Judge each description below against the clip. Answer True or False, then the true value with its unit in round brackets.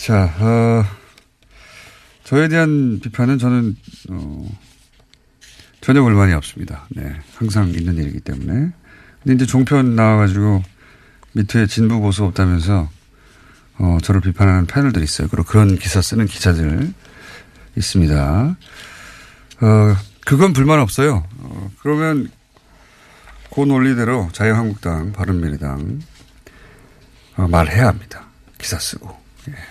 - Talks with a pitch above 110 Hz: False (105 Hz)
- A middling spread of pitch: False (5.7 semitones)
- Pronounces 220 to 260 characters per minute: True (240 characters per minute)